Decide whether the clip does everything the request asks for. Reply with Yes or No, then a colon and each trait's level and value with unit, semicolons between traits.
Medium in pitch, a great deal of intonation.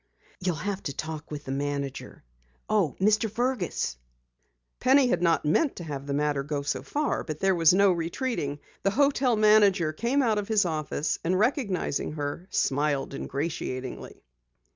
Yes: medium, 170 Hz; wide, 6.7 semitones